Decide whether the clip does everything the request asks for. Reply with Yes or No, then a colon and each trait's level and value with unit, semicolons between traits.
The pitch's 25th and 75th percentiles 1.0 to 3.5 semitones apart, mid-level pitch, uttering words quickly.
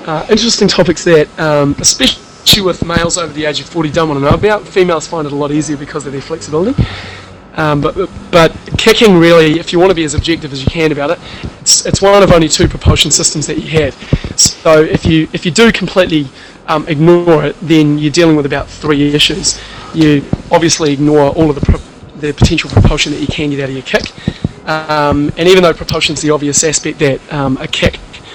Yes: narrow, 2.4 semitones; medium, 155 Hz; fast, 215 wpm